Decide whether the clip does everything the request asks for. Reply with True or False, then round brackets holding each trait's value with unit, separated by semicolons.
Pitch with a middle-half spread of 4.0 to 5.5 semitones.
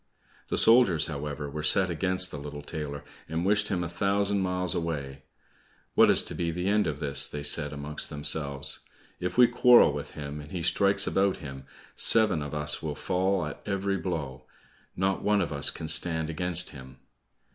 True (4.7 semitones)